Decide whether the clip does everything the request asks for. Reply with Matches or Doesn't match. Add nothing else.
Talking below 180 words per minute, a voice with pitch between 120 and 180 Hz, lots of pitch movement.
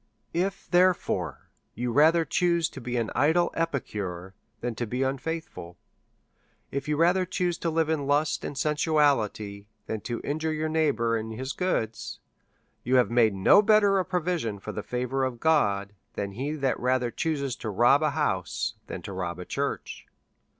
Matches